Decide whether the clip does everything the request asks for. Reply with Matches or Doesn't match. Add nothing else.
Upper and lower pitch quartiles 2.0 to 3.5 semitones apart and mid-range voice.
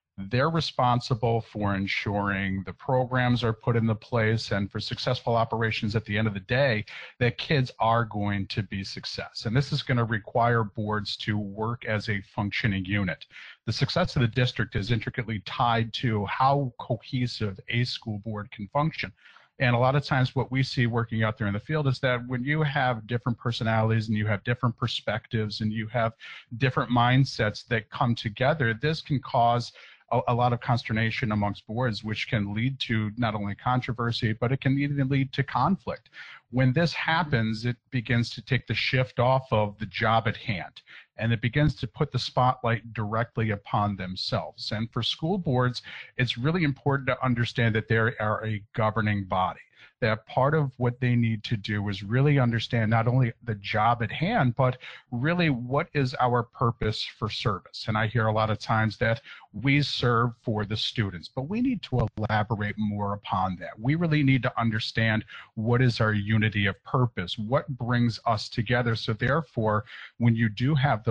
Doesn't match